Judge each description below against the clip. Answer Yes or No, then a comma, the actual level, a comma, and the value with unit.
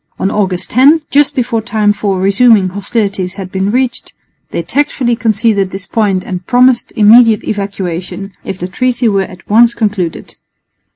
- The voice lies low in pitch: No, high, 210 Hz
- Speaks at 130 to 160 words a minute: Yes, average, 155 wpm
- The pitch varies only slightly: No, average, 3.7 semitones